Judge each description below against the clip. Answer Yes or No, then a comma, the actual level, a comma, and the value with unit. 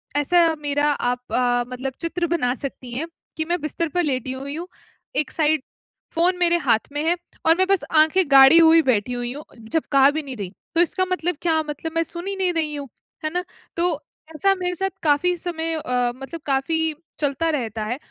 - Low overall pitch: No, very high, 310 Hz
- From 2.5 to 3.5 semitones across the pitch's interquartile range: No, average, 4.2 semitones